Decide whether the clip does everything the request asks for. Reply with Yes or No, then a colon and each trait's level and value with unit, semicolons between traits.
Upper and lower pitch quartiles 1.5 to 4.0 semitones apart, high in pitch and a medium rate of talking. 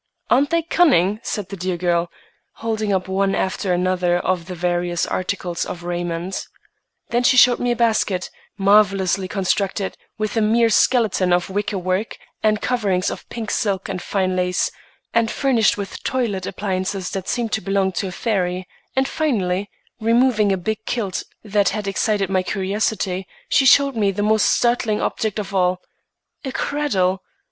Yes: average, 3.2 semitones; high, 195 Hz; average, 160 wpm